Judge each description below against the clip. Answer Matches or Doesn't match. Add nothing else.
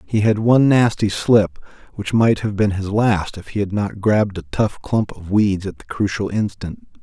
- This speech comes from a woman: Doesn't match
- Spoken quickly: Matches